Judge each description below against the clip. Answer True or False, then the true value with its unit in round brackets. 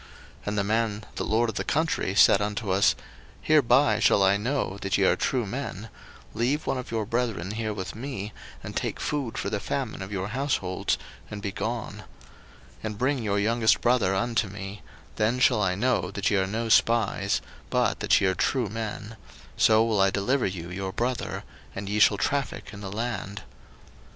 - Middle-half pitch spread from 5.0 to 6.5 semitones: False (3.2 semitones)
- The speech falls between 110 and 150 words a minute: False (195 wpm)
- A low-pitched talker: True (105 Hz)